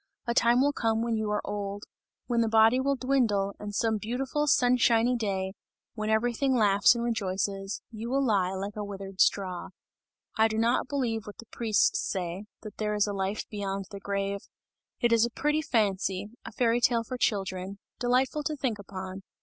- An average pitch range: Yes, average, 3.3 semitones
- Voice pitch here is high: Yes, high, 220 Hz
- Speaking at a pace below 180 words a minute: No, average, 185 wpm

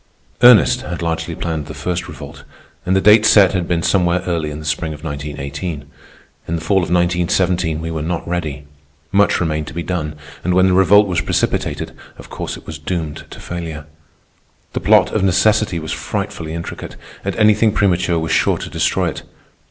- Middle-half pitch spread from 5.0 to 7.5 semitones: No, average, 3.0 semitones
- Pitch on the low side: Yes, very low, 85 Hz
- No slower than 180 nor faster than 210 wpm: Yes, average, 190 wpm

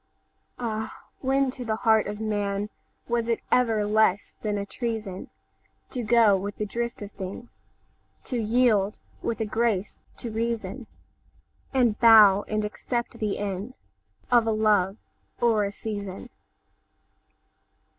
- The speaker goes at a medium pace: No, slow, 115 wpm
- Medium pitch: No, high, 220 Hz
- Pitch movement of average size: No, narrow, 2.3 semitones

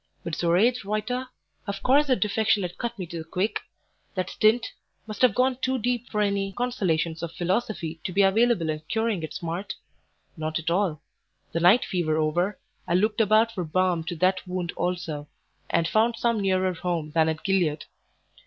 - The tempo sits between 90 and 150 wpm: No, average, 180 wpm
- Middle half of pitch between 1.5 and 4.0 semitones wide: No, average, 4.6 semitones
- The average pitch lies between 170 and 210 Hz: Yes, medium, 185 Hz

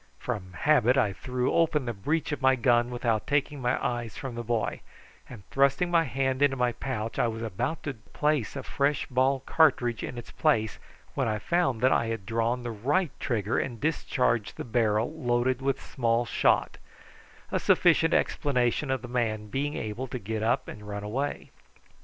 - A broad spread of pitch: No, average, 3.2 semitones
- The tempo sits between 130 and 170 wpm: No, average, 185 wpm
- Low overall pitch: Yes, low, 125 Hz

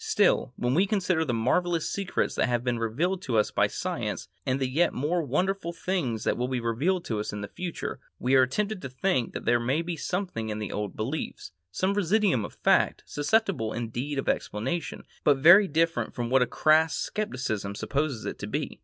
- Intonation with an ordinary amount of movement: No, wide, 6.9 semitones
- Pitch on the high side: No, medium, 140 Hz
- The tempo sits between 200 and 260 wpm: Yes, fast, 205 wpm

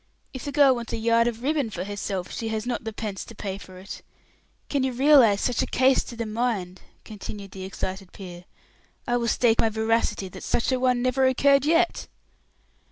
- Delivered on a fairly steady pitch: No, average, 4.1 semitones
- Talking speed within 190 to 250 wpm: Yes, fast, 205 wpm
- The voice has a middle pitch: No, high, 230 Hz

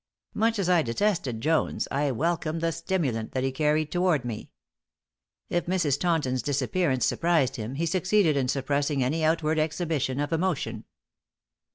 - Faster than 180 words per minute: No, average, 150 wpm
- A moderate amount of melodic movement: Yes, average, 4.3 semitones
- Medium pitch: Yes, medium, 155 Hz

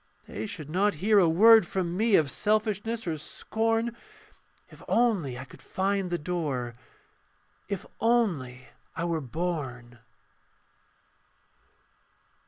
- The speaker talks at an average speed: No, slow, 115 wpm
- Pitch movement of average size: No, wide, 6.5 semitones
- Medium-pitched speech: Yes, medium, 180 Hz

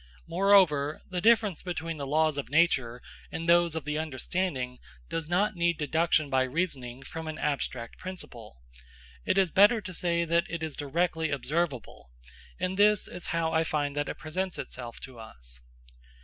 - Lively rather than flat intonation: No, average, 3.8 semitones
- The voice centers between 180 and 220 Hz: No, medium, 160 Hz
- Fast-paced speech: No, average, 165 wpm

